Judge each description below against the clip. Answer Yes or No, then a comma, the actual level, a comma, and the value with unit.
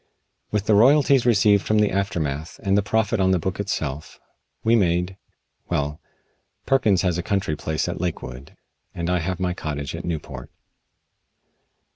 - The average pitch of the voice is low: Yes, very low, 95 Hz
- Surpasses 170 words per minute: No, average, 155 wpm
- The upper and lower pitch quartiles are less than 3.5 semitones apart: No, average, 4.3 semitones